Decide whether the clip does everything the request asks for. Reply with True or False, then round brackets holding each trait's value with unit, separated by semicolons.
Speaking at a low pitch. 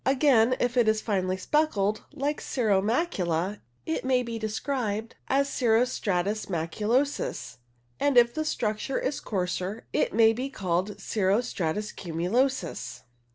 False (220 Hz)